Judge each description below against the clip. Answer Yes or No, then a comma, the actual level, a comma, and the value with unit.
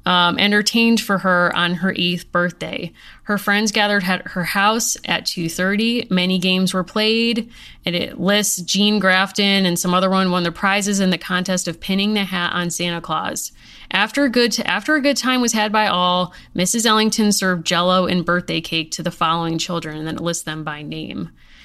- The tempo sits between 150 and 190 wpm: No, average, 200 wpm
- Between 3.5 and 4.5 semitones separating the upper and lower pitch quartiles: No, average, 3.1 semitones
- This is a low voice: No, medium, 185 Hz